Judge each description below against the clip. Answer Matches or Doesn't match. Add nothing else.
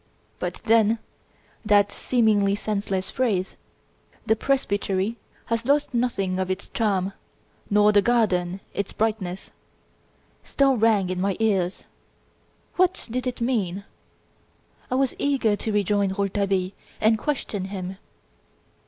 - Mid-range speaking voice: Doesn't match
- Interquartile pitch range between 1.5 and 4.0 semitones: Matches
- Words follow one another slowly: Matches